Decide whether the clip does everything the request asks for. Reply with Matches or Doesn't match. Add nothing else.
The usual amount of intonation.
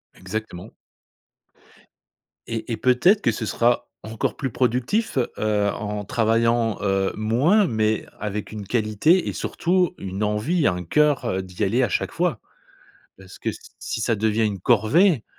Matches